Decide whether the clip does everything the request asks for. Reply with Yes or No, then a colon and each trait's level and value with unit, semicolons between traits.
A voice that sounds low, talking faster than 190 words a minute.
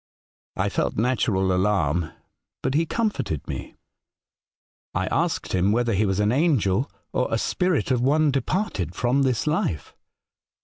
No: low, 120 Hz; average, 140 wpm